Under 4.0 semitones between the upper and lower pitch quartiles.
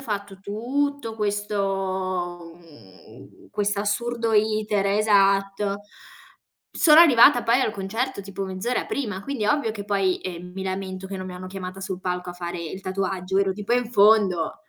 Yes: narrow, 2.5 semitones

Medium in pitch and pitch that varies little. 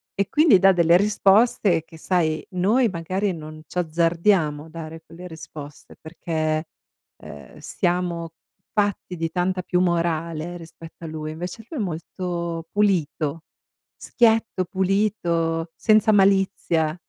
No: medium, 175 Hz; average, 3.0 semitones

